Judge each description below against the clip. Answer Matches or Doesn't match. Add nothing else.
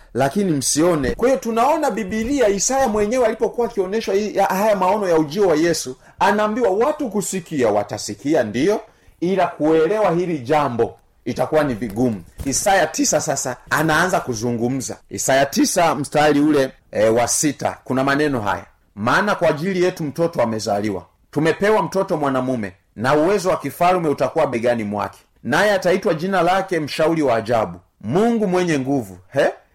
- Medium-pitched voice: Matches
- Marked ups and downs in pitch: Matches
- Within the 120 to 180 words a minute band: Matches